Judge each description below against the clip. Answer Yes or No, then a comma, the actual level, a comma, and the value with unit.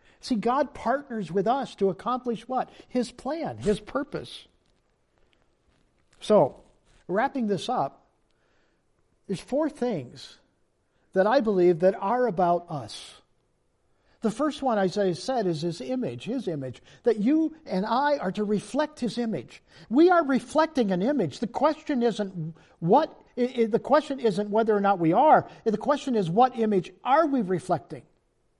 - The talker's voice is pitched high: Yes, high, 225 Hz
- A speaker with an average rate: Yes, average, 145 wpm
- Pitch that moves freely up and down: Yes, wide, 5.9 semitones